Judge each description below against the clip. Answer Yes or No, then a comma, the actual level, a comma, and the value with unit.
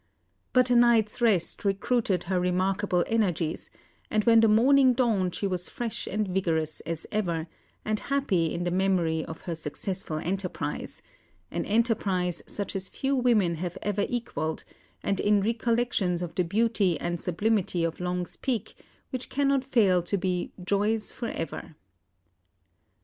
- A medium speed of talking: Yes, average, 150 wpm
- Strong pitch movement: No, average, 4.3 semitones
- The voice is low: No, high, 195 Hz